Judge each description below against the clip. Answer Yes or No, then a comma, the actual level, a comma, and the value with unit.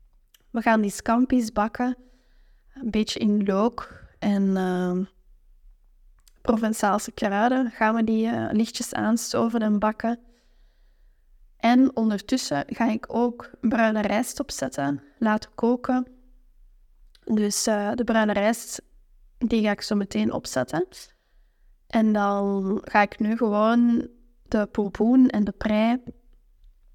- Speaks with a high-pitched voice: Yes, high, 220 Hz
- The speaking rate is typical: No, slow, 120 wpm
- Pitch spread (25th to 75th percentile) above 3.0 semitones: No, narrow, 2.6 semitones